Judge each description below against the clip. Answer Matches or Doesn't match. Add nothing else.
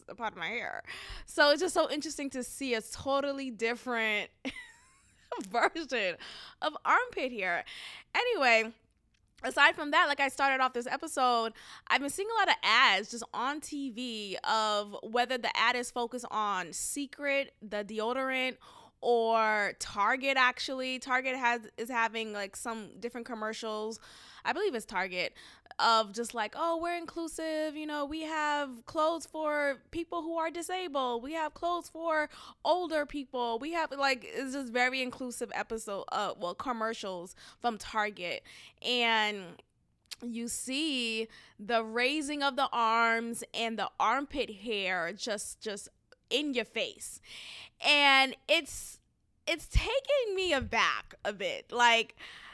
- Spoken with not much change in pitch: Doesn't match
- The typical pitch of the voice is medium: Doesn't match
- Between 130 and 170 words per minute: Matches